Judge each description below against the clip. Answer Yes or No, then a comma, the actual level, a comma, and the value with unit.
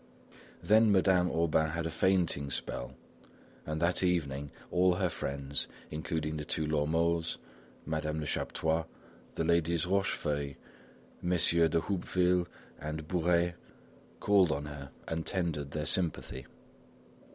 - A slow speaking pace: Yes, slow, 120 wpm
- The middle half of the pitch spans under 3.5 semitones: Yes, narrow, 2.6 semitones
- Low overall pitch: Yes, very low, 80 Hz